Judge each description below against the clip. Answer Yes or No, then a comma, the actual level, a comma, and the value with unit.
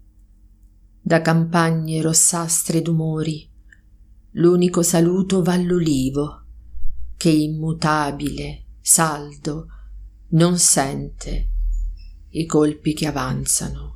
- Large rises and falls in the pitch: Yes, wide, 8.4 semitones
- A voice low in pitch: No, medium, 155 Hz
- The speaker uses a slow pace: Yes, slow, 75 wpm